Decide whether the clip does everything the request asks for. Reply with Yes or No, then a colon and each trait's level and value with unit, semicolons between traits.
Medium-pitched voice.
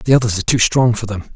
No: low, 115 Hz